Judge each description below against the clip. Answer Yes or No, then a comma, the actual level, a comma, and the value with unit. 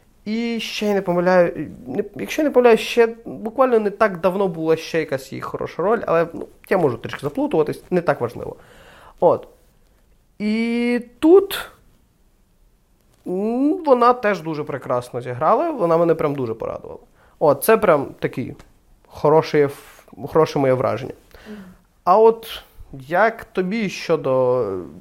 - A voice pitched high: Yes, high, 195 Hz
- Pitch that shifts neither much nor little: No, wide, 6.6 semitones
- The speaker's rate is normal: Yes, average, 130 wpm